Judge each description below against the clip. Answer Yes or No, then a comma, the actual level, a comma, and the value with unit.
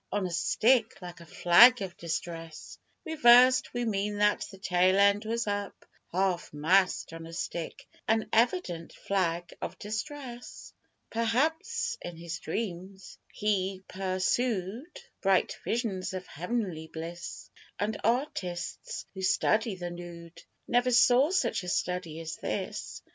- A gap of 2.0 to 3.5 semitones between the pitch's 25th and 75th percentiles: No, average, 5.0 semitones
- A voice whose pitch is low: No, high, 195 Hz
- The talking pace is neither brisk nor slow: No, slow, 130 wpm